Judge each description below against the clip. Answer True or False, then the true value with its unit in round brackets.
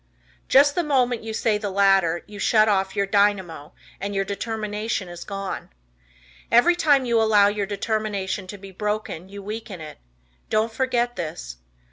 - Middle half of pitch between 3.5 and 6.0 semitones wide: False (2.5 semitones)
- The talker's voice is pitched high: True (205 Hz)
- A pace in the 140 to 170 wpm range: True (160 wpm)